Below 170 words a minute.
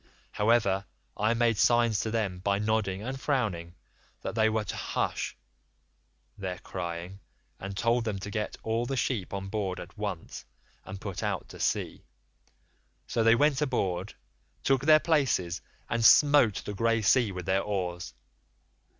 Yes: average, 155 wpm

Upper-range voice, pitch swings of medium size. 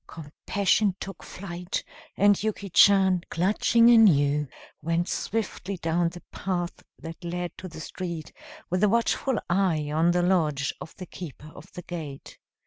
No: medium, 175 Hz; average, 3.1 semitones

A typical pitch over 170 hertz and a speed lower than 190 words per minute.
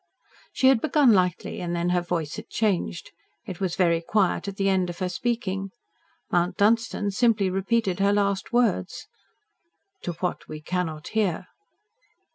Yes: high, 190 Hz; average, 155 wpm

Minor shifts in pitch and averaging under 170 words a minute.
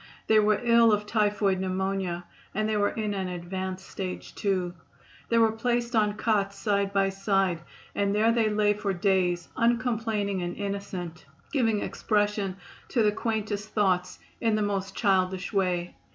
Yes: narrow, 2.2 semitones; average, 155 wpm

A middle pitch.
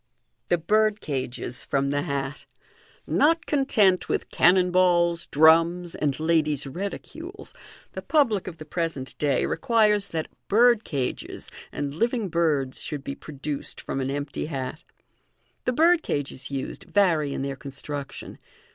Yes: medium, 160 Hz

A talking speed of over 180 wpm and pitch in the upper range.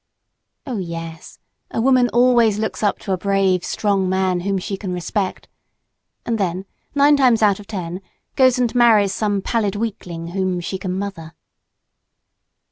No: average, 155 wpm; high, 200 Hz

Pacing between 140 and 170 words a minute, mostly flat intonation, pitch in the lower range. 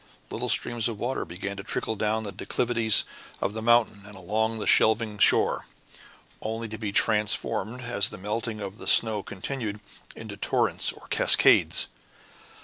Yes: average, 155 wpm; narrow, 2.0 semitones; low, 110 Hz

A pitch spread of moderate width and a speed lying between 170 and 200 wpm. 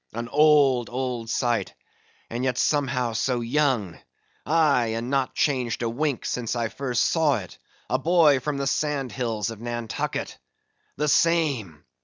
No: average, 3.7 semitones; average, 150 wpm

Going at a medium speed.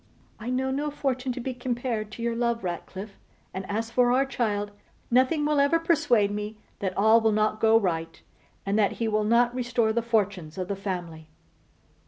Yes: average, 190 wpm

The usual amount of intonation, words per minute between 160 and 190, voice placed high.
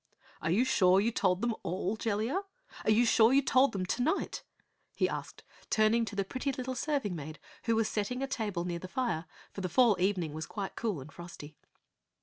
No: average, 5.0 semitones; average, 200 wpm; high, 210 Hz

